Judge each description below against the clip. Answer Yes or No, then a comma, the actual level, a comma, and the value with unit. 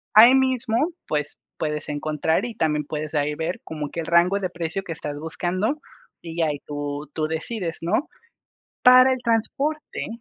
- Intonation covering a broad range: Yes, wide, 6.8 semitones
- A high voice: No, medium, 165 Hz